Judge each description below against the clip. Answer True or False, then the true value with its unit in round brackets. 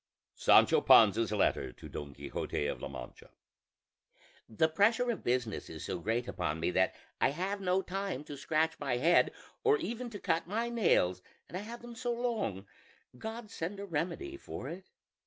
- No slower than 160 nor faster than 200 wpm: True (175 wpm)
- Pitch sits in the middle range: True (170 Hz)